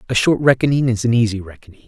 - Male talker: Yes, male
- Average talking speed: No, fast, 225 wpm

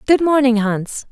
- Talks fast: No, average, 160 wpm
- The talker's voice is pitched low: No, very high, 250 Hz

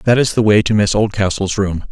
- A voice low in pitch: Yes, low, 105 Hz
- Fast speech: Yes, fast, 250 wpm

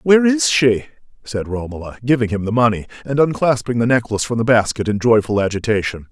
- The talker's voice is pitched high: No, low, 120 Hz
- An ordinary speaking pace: Yes, average, 185 wpm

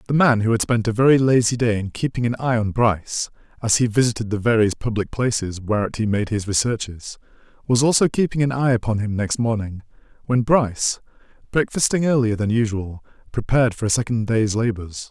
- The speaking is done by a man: Yes, male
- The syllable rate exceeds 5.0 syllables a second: Yes, 5.7 syllables/s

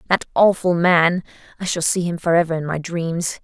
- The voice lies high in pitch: No, medium, 170 Hz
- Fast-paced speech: No, average, 190 wpm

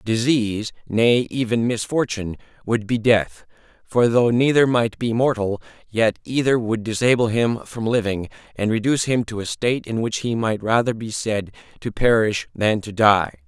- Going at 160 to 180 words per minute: Yes, average, 170 wpm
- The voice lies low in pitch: Yes, low, 110 Hz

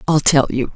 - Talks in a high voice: No, medium, 145 Hz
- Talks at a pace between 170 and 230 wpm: No, fast, 240 wpm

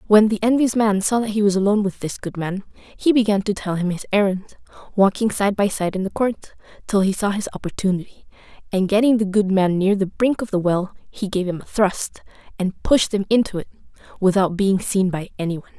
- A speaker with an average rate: No, fast, 225 wpm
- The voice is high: Yes, high, 200 Hz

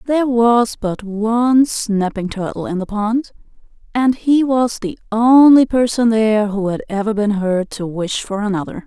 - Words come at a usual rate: Yes, average, 170 wpm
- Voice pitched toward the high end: Yes, high, 220 Hz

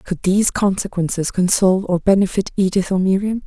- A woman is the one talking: Yes, female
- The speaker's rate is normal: Yes, average, 155 wpm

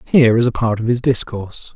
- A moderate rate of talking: No, fast, 240 wpm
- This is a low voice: Yes, low, 115 Hz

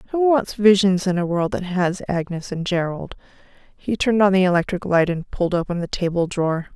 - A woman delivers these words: Yes, female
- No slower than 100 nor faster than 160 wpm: No, fast, 205 wpm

